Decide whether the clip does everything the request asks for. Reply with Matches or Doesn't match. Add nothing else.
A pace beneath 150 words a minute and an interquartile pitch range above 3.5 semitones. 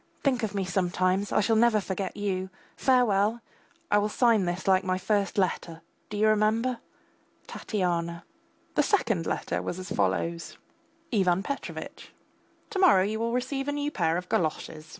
Doesn't match